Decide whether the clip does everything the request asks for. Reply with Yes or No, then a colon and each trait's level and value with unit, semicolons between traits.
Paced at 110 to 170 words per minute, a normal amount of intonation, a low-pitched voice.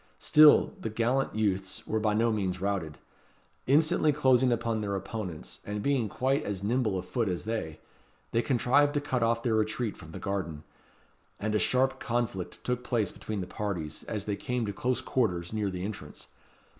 No: average, 180 wpm; average, 4.0 semitones; low, 110 Hz